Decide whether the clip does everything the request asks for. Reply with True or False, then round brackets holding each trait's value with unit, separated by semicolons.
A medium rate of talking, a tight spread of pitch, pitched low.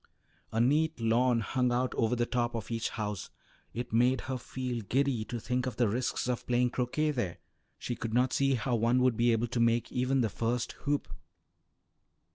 True (195 wpm; 1.6 semitones; 120 Hz)